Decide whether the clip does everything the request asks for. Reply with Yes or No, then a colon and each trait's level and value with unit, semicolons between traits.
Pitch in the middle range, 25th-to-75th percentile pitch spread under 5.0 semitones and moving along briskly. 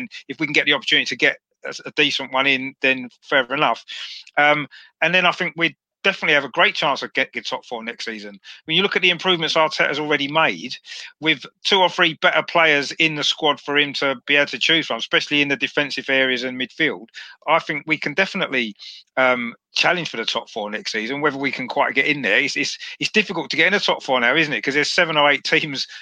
Yes: medium, 150 Hz; average, 3.4 semitones; fast, 245 wpm